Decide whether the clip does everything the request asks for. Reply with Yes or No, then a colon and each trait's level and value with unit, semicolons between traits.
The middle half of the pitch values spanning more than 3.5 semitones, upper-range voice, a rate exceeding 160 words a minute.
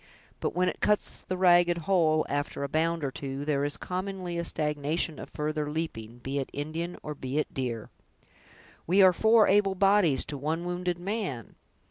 No: average, 4.1 semitones; medium, 160 Hz; average, 180 wpm